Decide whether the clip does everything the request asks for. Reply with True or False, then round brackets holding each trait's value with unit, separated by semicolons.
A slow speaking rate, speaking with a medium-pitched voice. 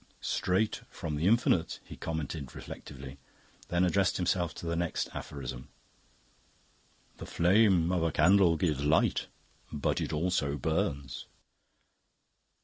False (120 wpm; 85 Hz)